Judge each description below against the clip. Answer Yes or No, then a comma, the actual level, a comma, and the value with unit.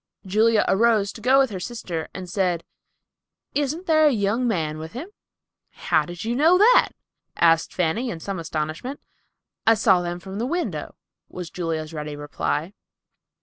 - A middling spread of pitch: No, wide, 6.6 semitones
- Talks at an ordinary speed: Yes, average, 160 wpm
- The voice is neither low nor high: No, high, 195 Hz